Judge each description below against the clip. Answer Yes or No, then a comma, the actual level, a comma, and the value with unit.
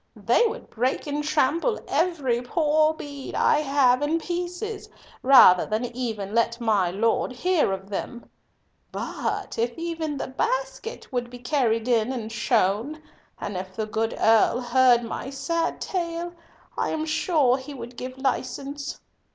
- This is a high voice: Yes, very high, 260 Hz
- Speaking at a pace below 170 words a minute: Yes, average, 150 wpm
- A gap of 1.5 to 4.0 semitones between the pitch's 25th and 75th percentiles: No, average, 5.1 semitones